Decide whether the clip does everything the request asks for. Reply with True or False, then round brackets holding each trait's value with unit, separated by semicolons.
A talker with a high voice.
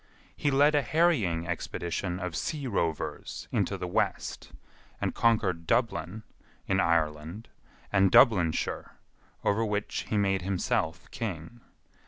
False (95 Hz)